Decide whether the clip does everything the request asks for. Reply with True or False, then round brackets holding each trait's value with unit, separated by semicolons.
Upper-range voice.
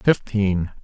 False (100 Hz)